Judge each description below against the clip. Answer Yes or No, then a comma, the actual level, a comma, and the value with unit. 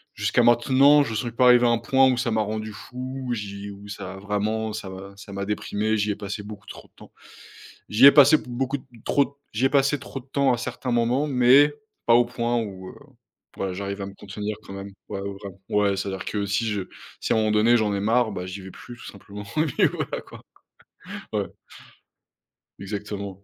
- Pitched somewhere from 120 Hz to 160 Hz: No, low, 110 Hz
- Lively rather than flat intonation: No, average, 3.7 semitones